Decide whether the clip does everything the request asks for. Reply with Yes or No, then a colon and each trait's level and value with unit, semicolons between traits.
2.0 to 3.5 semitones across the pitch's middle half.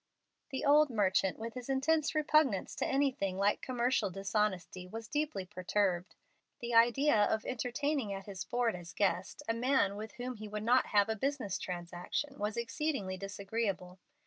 No: average, 5.1 semitones